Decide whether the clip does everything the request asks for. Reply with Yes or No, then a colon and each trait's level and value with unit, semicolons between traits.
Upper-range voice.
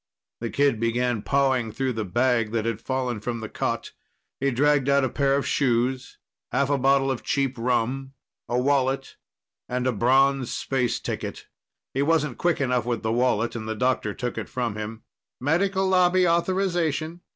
No: low, 130 Hz